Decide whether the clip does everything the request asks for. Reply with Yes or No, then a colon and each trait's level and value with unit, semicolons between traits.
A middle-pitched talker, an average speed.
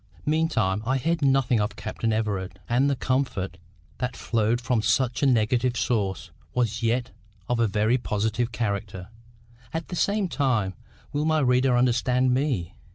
No: low, 120 Hz; average, 150 wpm